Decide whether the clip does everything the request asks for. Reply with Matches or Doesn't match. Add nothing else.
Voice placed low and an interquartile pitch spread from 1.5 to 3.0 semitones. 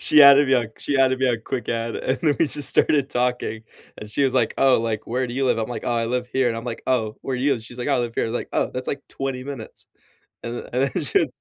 Matches